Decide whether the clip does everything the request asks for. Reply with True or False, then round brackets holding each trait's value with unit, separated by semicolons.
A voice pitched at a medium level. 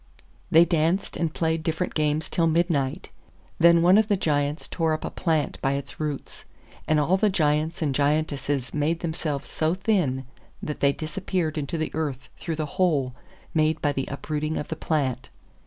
True (155 Hz)